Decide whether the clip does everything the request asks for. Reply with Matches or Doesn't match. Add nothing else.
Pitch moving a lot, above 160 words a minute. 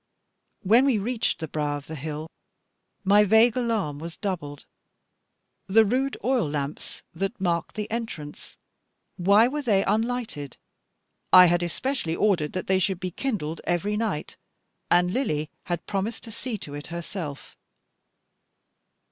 Doesn't match